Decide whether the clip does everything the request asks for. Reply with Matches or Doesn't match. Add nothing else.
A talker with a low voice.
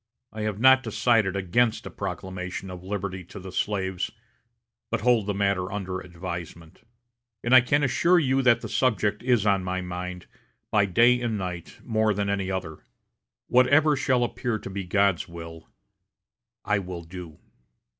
Matches